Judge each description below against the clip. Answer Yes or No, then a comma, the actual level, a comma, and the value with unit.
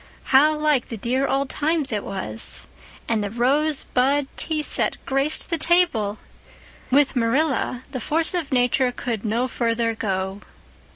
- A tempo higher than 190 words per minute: No, average, 150 wpm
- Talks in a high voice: Yes, very high, 260 Hz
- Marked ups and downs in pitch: No, average, 4.5 semitones